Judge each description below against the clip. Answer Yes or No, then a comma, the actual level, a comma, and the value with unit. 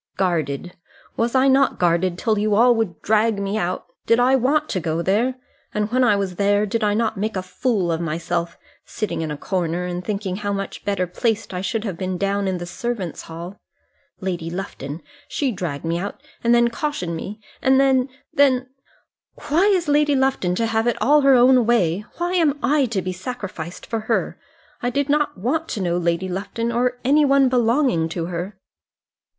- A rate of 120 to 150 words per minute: No, average, 195 wpm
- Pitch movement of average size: No, wide, 5.7 semitones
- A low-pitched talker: No, high, 210 Hz